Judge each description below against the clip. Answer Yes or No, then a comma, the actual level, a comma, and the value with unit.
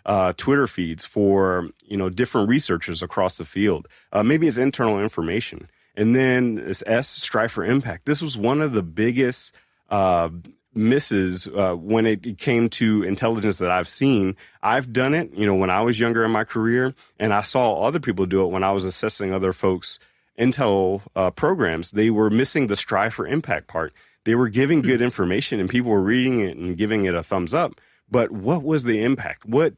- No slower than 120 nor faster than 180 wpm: No, average, 195 wpm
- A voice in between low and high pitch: No, low, 110 Hz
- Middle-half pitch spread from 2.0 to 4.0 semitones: No, average, 4.4 semitones